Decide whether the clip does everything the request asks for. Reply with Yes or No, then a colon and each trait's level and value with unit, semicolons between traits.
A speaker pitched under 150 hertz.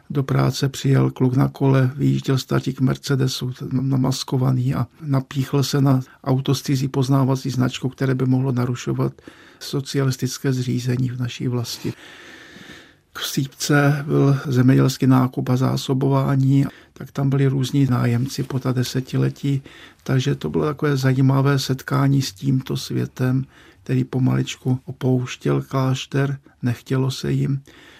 Yes: low, 135 Hz